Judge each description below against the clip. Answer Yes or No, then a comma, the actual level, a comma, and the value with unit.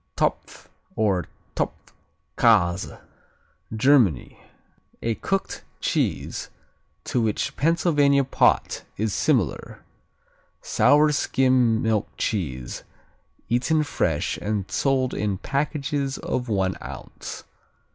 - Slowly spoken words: Yes, slow, 85 wpm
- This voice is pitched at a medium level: No, low, 120 Hz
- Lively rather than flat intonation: Yes, wide, 5.7 semitones